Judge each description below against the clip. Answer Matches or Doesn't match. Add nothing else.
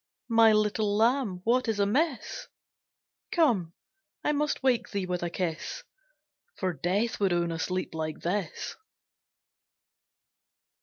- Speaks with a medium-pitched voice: Doesn't match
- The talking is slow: Matches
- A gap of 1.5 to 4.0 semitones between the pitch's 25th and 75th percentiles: Doesn't match